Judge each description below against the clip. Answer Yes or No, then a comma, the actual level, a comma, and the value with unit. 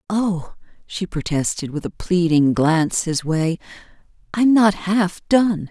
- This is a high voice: No, medium, 180 Hz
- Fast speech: No, slow, 135 wpm